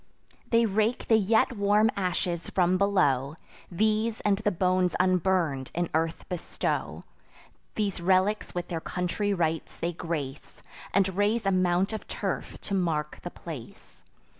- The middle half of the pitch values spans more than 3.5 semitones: No, average, 3.1 semitones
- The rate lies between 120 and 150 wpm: Yes, average, 140 wpm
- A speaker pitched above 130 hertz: Yes, medium, 185 Hz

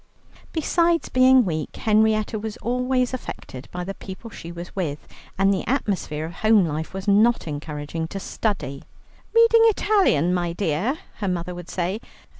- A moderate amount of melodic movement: No, wide, 6.1 semitones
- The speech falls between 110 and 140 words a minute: No, average, 155 wpm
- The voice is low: No, high, 195 Hz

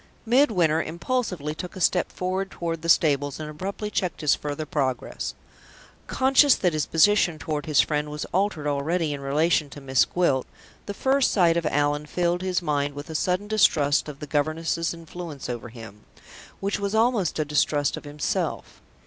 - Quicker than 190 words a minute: No, average, 175 wpm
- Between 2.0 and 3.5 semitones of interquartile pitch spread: No, average, 3.9 semitones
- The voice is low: No, medium, 160 Hz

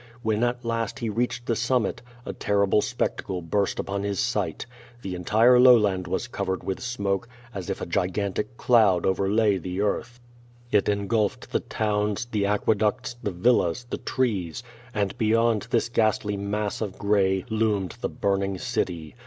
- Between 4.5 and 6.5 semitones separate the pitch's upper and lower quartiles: No, average, 2.9 semitones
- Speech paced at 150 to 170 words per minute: Yes, average, 160 wpm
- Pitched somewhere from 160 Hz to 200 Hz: No, low, 105 Hz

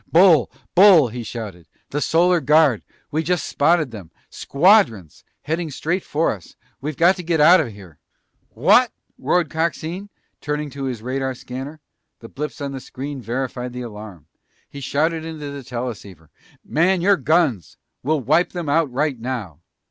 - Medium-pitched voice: Yes, medium, 145 Hz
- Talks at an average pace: Yes, average, 160 wpm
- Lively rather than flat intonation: No, average, 5.0 semitones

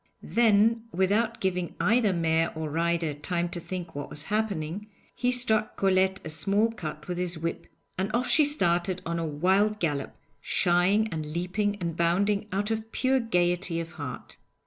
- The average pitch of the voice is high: No, medium, 180 Hz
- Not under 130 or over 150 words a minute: No, average, 170 wpm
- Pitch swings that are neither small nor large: Yes, average, 4.0 semitones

